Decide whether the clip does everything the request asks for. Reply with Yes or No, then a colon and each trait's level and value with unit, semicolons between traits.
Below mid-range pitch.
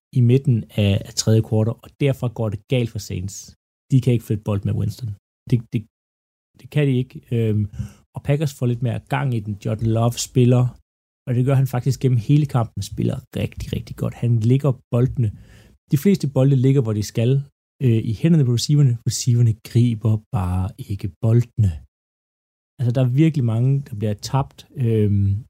Yes: low, 120 Hz